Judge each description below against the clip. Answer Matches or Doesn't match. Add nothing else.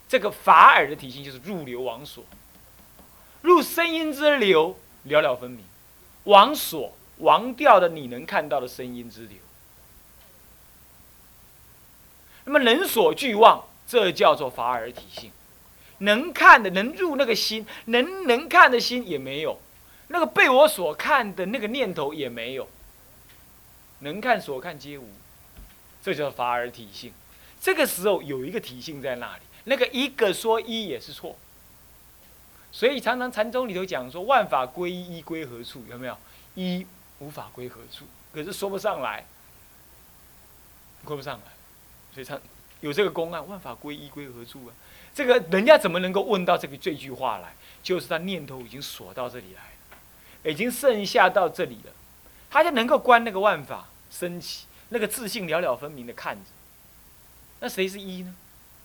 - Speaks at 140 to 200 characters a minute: Doesn't match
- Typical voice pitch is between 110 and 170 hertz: Doesn't match